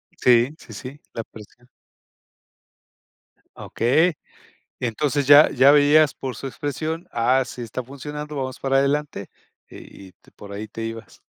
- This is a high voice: No, low, 135 Hz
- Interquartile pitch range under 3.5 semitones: No, average, 3.9 semitones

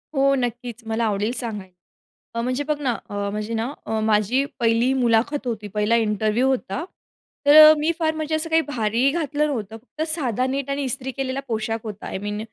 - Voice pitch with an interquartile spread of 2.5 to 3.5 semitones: No, average, 4.2 semitones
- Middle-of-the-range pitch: No, high, 245 Hz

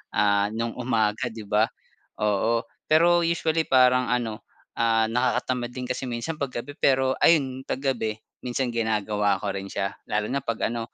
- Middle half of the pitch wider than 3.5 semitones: No, average, 3.1 semitones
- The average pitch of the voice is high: No, low, 120 Hz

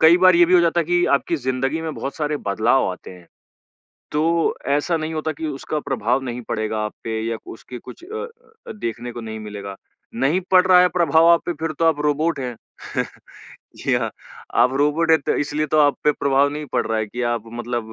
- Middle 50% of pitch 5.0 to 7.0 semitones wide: Yes, average, 5.3 semitones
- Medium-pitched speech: Yes, medium, 145 Hz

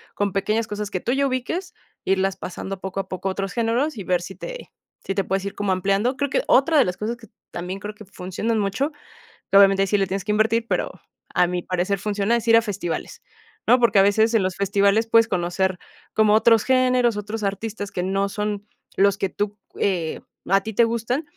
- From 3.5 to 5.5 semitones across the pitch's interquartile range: No, average, 2.8 semitones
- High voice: Yes, high, 205 Hz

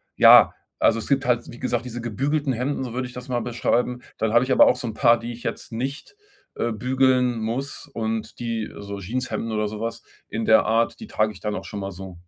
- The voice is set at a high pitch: No, low, 120 Hz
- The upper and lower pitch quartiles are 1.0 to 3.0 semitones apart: Yes, narrow, 2.4 semitones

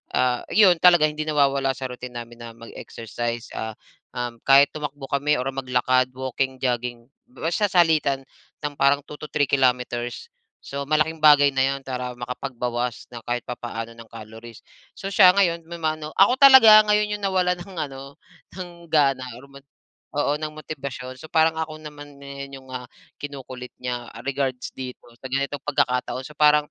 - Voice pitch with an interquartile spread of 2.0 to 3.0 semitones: No, average, 3.6 semitones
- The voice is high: No, medium, 140 Hz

